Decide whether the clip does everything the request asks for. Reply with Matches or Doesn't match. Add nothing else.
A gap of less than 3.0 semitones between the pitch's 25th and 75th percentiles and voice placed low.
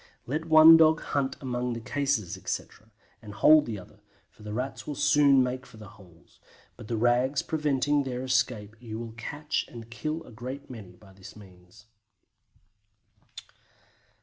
Doesn't match